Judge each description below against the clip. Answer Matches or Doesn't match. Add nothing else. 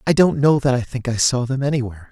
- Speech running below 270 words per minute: Doesn't match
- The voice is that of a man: Matches